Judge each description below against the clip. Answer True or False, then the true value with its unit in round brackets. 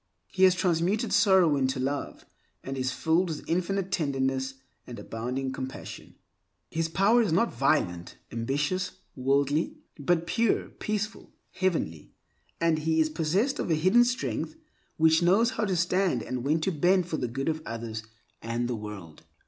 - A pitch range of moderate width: False (5.9 semitones)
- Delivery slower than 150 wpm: False (155 wpm)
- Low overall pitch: False (160 Hz)